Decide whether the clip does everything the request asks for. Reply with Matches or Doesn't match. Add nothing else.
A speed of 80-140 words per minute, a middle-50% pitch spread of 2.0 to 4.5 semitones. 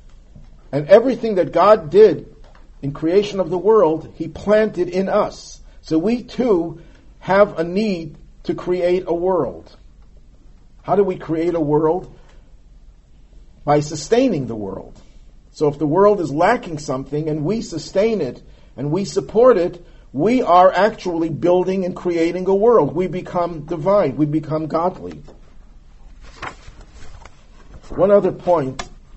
Matches